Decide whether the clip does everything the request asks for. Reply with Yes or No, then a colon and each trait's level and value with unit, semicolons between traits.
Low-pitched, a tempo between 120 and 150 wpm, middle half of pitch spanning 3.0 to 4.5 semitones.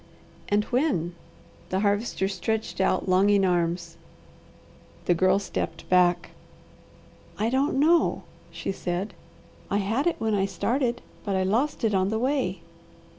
No: high, 205 Hz; slow, 135 wpm; average, 4.2 semitones